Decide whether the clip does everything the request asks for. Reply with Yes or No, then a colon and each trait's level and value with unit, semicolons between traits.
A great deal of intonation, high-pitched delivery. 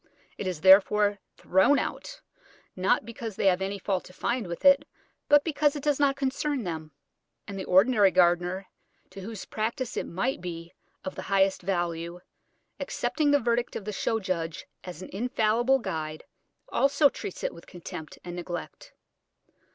Yes: wide, 5.9 semitones; high, 195 Hz